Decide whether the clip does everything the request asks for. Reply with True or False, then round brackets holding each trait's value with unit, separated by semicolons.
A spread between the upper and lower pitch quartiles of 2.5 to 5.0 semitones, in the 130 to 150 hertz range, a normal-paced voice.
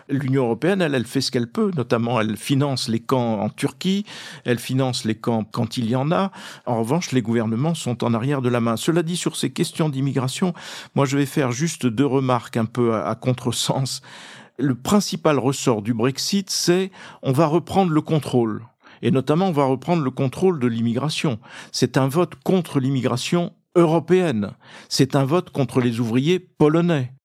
False (5.5 semitones; 135 Hz; 180 wpm)